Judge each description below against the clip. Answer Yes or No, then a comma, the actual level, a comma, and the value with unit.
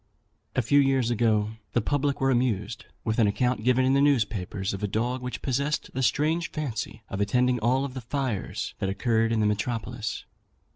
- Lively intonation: No, average, 3.5 semitones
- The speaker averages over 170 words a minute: Yes, average, 185 wpm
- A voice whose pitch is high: No, low, 120 Hz